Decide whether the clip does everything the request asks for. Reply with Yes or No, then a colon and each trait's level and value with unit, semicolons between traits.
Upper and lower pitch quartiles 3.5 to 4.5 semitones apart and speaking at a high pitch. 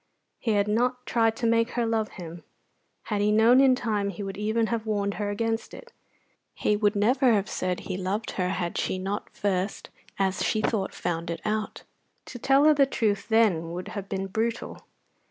No: average, 2.9 semitones; high, 210 Hz